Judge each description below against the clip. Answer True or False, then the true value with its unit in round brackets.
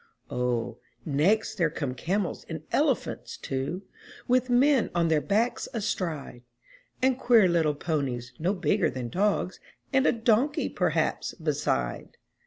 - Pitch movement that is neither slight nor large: False (7.4 semitones)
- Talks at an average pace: False (130 wpm)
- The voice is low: False (180 Hz)